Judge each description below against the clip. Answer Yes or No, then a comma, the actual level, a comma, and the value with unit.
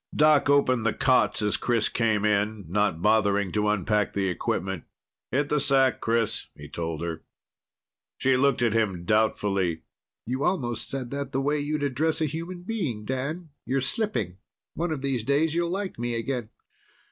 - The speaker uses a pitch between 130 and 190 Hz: No, low, 120 Hz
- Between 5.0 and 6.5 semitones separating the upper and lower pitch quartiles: Yes, wide, 5.4 semitones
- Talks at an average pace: Yes, average, 170 wpm